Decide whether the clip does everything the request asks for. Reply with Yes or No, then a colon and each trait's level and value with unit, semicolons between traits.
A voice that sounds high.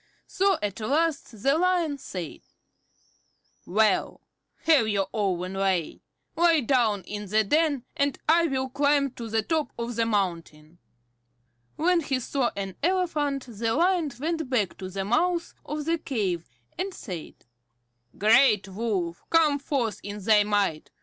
Yes: high, 235 Hz